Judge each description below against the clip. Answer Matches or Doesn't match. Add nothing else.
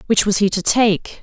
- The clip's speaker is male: Doesn't match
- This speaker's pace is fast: Matches